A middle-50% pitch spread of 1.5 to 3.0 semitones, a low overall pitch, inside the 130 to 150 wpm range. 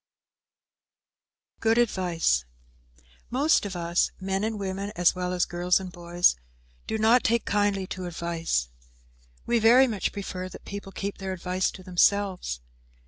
No: average, 2.7 semitones; high, 190 Hz; average, 145 wpm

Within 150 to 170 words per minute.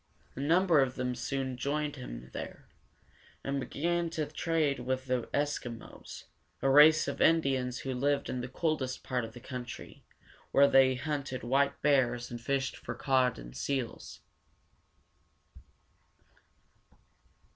No: slow, 135 wpm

